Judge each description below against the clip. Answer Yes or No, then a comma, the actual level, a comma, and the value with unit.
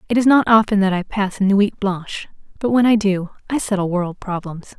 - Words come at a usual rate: No, fast, 225 wpm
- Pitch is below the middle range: No, high, 205 Hz